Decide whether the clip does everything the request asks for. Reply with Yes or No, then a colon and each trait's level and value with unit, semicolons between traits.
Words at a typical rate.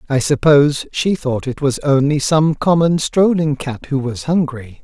Yes: average, 175 wpm